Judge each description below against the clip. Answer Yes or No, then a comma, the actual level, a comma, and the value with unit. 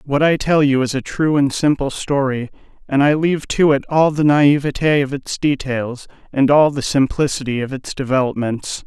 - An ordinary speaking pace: Yes, average, 190 wpm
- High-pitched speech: No, medium, 140 Hz